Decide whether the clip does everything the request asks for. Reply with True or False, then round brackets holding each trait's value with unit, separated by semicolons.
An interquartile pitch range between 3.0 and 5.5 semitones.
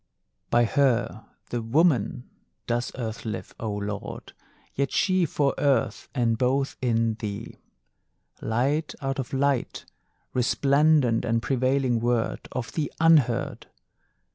True (3.3 semitones)